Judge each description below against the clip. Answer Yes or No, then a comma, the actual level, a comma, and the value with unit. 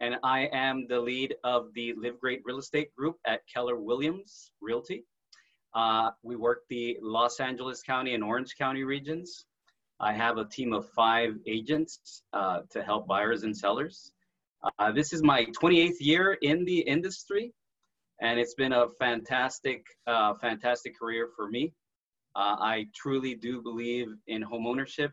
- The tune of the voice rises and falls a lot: No, average, 3.1 semitones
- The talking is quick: No, average, 160 wpm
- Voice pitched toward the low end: Yes, low, 120 Hz